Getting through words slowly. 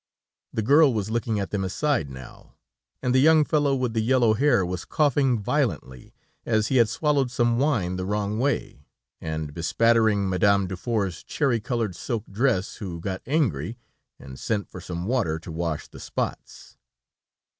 No: average, 165 wpm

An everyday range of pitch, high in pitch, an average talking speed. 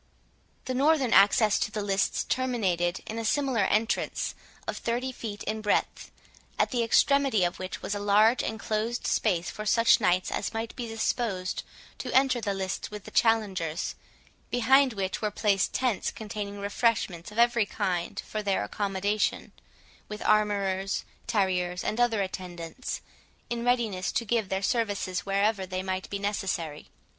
Yes: average, 3.2 semitones; high, 210 Hz; average, 155 wpm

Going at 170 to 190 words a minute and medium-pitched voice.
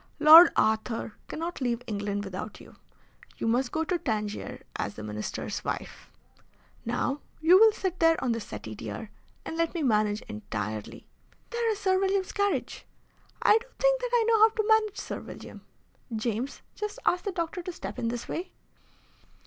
No: average, 175 wpm; very high, 320 Hz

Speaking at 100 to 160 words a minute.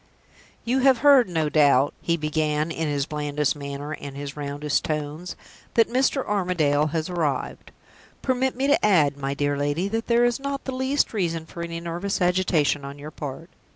No: average, 180 wpm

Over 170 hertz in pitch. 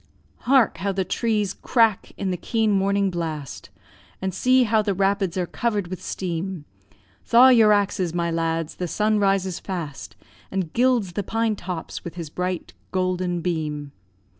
Yes: high, 190 Hz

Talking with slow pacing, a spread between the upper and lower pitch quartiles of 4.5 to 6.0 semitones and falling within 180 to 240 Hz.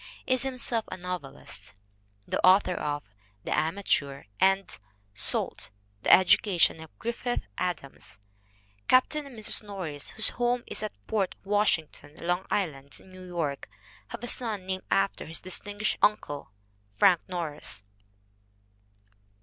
Yes: slow, 125 wpm; average, 4.8 semitones; medium, 185 Hz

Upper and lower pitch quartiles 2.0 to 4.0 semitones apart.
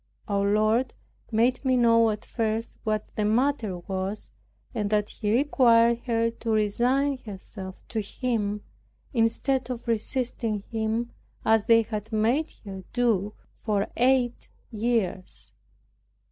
Yes: narrow, 2.5 semitones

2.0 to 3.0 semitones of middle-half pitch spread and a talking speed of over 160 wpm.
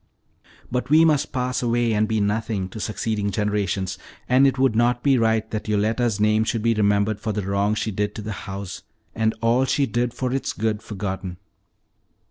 Yes: average, 2.7 semitones; average, 190 wpm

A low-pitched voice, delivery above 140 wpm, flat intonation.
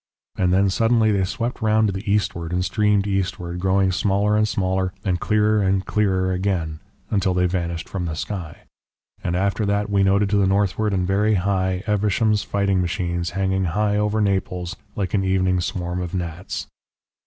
Yes: very low, 95 Hz; average, 175 wpm; narrow, 2.2 semitones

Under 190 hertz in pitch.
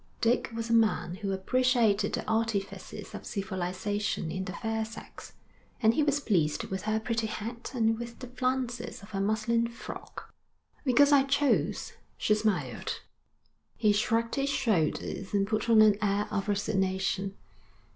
No: high, 220 Hz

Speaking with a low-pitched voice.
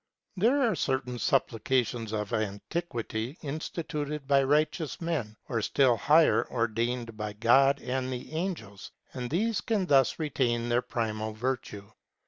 Yes: low, 130 Hz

